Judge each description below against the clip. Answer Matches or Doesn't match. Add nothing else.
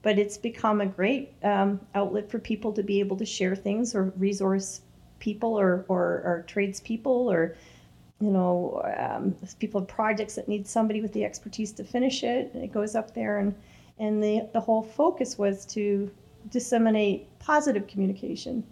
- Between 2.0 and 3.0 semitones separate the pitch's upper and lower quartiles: Matches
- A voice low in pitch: Doesn't match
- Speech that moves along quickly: Doesn't match